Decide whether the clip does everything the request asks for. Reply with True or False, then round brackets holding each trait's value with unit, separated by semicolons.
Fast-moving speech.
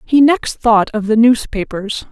False (170 wpm)